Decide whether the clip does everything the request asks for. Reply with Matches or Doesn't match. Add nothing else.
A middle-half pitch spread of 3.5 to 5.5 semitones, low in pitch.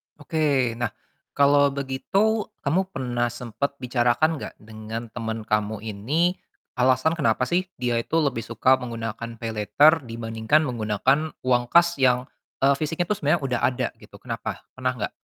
Matches